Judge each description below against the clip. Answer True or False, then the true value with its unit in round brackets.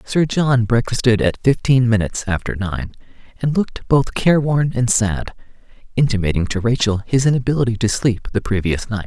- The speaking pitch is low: True (115 Hz)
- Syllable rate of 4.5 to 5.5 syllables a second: True (5.4 syllables/s)